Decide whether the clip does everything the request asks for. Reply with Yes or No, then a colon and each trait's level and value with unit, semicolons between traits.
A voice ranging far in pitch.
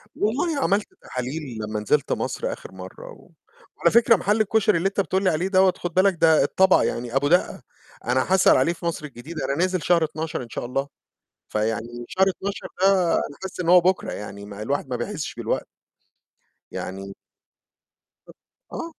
Yes: wide, 7.4 semitones